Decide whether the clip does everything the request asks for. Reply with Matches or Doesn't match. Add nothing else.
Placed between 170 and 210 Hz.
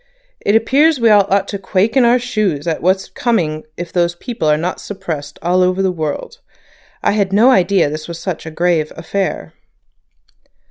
Matches